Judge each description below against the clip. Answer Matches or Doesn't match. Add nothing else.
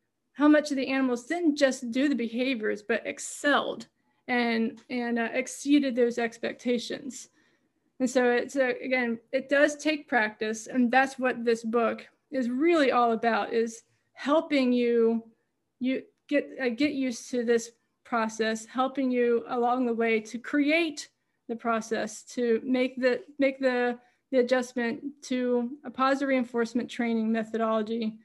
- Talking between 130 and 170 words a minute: Matches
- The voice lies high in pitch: Matches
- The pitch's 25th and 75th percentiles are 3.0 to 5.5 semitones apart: Doesn't match